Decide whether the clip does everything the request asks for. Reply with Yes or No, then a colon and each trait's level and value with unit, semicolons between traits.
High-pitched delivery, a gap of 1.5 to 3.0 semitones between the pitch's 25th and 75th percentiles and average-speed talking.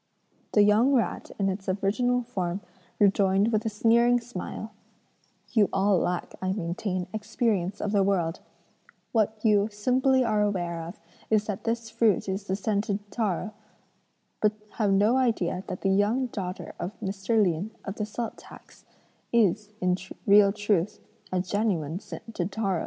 Yes: high, 205 Hz; narrow, 2.6 semitones; average, 150 wpm